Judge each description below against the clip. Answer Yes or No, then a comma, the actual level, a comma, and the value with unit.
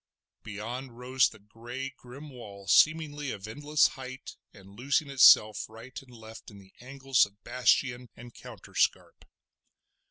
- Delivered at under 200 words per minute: Yes, slow, 135 wpm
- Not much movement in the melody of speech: No, average, 3.7 semitones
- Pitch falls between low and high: No, low, 125 Hz